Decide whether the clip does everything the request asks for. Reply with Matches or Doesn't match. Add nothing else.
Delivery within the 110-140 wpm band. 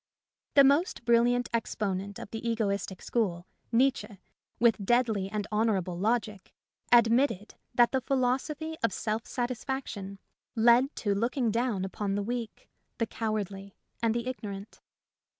Matches